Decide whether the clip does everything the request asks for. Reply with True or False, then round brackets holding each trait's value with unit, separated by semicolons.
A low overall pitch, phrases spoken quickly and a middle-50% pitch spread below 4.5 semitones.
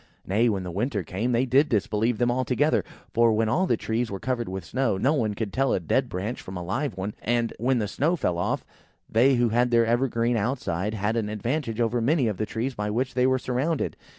True (115 Hz; 235 wpm; 3.4 semitones)